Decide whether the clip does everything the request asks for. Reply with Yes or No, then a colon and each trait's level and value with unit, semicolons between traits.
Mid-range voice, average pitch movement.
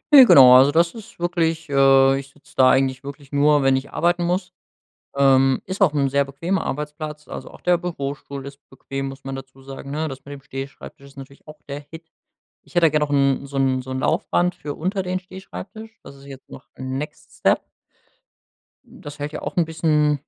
Yes: medium, 145 Hz; average, 3.3 semitones